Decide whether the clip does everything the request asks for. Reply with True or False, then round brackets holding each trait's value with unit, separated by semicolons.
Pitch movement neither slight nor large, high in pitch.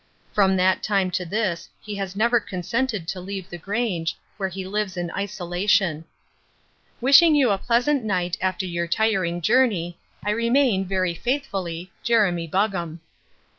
True (3.9 semitones; 195 Hz)